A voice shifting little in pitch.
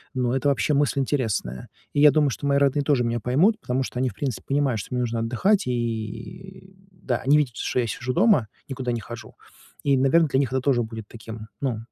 No: average, 3.5 semitones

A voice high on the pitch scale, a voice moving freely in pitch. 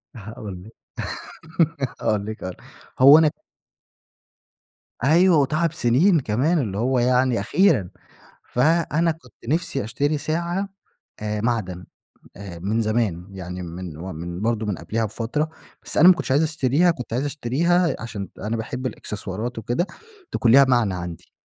No: low, 120 Hz; wide, 6.8 semitones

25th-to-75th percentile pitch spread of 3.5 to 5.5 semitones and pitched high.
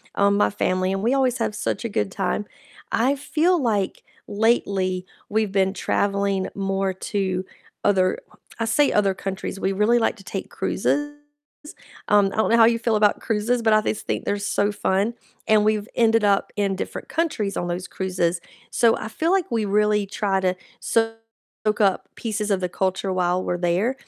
No: average, 2.8 semitones; high, 205 Hz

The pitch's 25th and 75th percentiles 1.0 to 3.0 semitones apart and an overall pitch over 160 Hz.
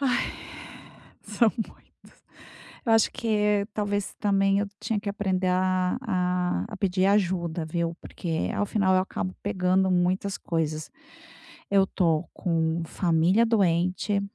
Yes: narrow, 2.4 semitones; high, 190 Hz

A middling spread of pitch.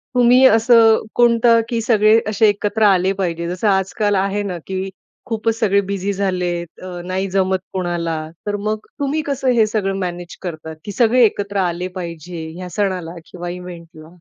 Yes: average, 3.6 semitones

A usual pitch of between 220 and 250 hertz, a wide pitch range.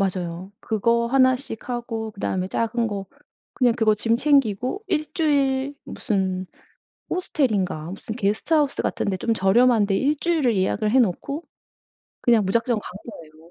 No: high, 230 Hz; average, 5.0 semitones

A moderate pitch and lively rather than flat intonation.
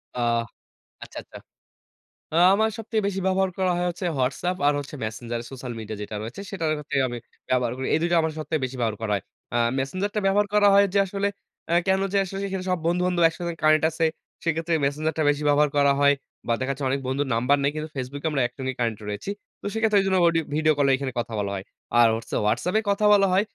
Yes: medium, 155 Hz; wide, 6.4 semitones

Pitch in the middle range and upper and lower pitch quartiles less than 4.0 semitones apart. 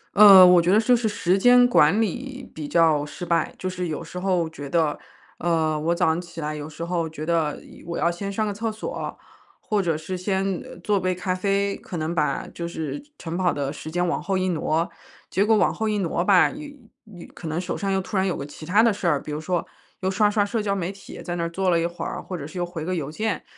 Yes: medium, 180 Hz; average, 3.5 semitones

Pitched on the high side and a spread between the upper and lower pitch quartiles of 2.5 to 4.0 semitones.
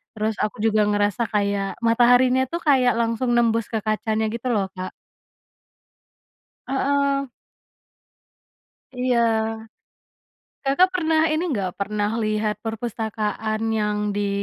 Yes: high, 225 Hz; average, 3.2 semitones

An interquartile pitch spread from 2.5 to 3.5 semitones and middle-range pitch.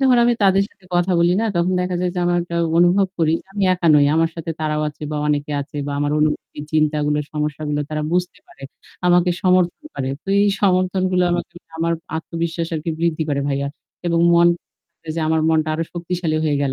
Yes: average, 2.9 semitones; medium, 170 Hz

